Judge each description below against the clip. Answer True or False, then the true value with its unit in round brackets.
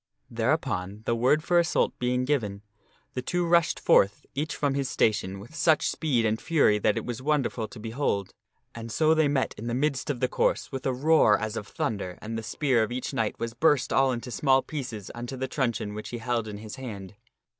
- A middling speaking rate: False (215 wpm)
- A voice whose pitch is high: False (125 Hz)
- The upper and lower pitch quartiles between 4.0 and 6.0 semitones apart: True (4.5 semitones)